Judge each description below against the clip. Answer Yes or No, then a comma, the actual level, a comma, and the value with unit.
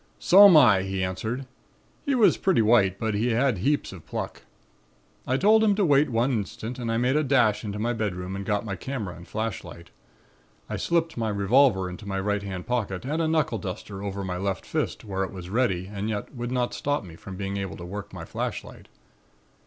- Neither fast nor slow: No, fast, 210 wpm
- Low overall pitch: Yes, low, 105 Hz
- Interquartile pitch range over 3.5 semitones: Yes, average, 5.0 semitones